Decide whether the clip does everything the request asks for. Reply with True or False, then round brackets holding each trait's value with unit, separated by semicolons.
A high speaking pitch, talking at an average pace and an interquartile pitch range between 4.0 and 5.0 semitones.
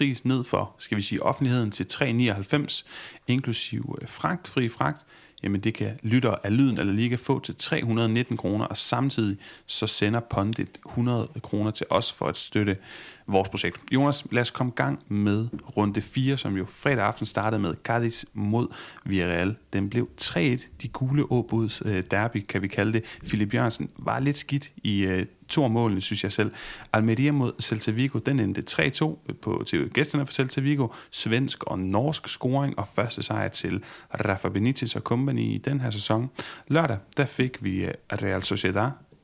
False (115 Hz; 175 wpm; 4.3 semitones)